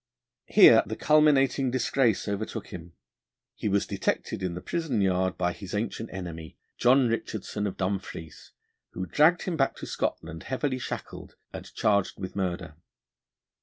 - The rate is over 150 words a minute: No, average, 145 wpm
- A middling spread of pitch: No, wide, 6.0 semitones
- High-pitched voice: No, low, 100 Hz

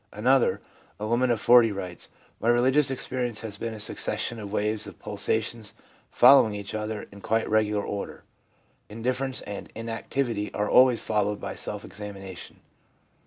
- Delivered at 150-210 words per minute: Yes, average, 165 wpm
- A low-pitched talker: Yes, low, 110 Hz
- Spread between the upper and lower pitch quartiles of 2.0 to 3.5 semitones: Yes, average, 2.7 semitones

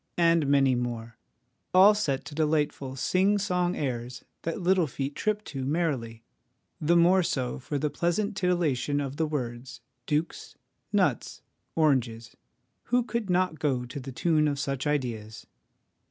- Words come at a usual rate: Yes, average, 150 wpm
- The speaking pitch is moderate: Yes, medium, 150 Hz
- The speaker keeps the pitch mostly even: No, average, 5.1 semitones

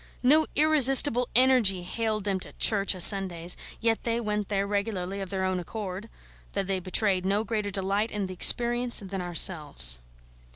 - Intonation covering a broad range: No, average, 3.4 semitones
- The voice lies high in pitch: Yes, high, 200 Hz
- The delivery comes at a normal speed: Yes, average, 165 wpm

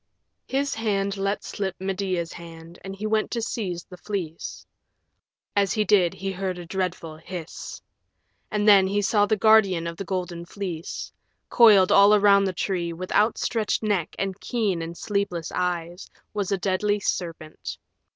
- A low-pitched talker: No, high, 195 Hz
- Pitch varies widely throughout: No, average, 2.8 semitones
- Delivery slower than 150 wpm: No, average, 160 wpm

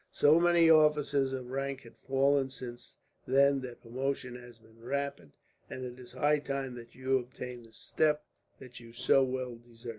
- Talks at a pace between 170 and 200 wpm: Yes, average, 175 wpm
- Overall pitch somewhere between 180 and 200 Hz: No, low, 130 Hz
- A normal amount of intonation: No, narrow, 2.3 semitones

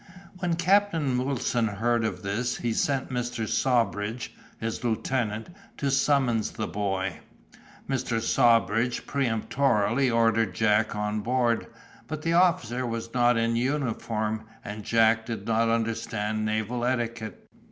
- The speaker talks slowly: Yes, slow, 125 wpm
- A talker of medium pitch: No, low, 115 Hz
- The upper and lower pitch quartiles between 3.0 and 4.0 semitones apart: No, narrow, 2.6 semitones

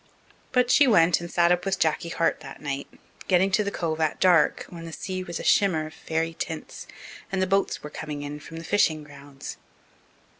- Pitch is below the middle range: No, medium, 165 Hz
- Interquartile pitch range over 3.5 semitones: No, average, 3.2 semitones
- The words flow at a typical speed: No, fast, 210 wpm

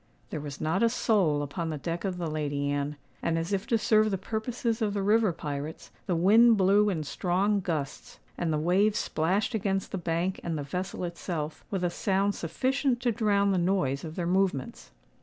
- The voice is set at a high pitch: No, medium, 180 Hz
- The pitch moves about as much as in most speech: Yes, average, 4.5 semitones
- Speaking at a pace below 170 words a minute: No, average, 200 wpm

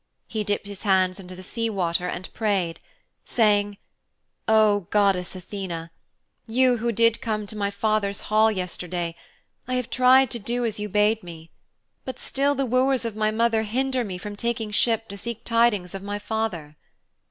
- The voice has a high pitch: Yes, high, 210 Hz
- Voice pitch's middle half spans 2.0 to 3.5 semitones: Yes, average, 3.2 semitones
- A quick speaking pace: No, average, 175 wpm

